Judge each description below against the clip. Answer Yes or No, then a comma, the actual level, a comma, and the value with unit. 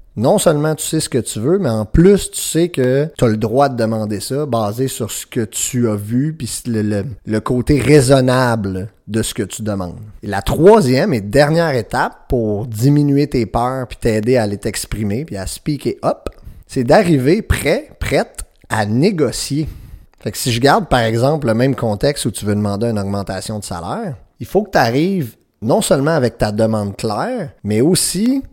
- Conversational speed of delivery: Yes, average, 200 wpm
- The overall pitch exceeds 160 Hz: No, low, 120 Hz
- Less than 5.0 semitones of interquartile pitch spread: No, average, 5.3 semitones